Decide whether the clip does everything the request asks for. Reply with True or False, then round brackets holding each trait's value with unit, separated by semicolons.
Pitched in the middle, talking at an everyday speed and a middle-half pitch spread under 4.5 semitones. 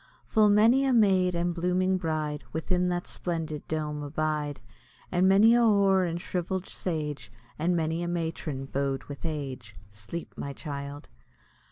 True (170 Hz; 150 wpm; 3.8 semitones)